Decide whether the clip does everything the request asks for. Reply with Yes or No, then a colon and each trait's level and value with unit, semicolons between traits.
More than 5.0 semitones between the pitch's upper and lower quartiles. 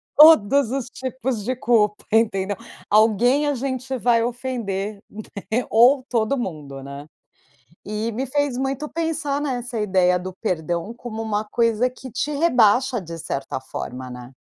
No: average, 4.5 semitones